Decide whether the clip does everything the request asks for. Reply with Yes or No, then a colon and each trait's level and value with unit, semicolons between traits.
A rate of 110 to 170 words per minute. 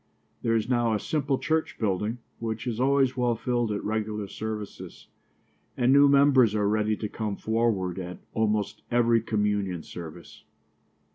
Yes: average, 150 wpm